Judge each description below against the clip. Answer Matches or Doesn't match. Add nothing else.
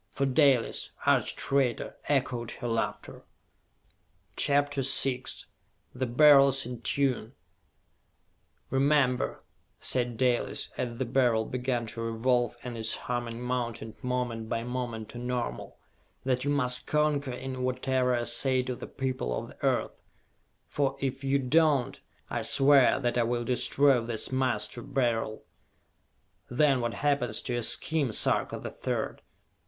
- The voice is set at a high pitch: Doesn't match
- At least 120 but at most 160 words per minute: Matches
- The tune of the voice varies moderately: Doesn't match